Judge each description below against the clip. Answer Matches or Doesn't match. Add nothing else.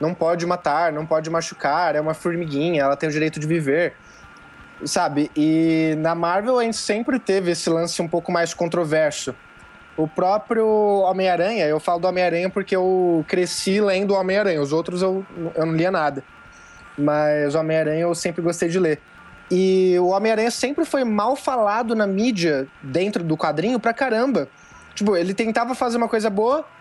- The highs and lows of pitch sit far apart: Doesn't match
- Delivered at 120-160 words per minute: Doesn't match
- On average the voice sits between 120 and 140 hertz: Doesn't match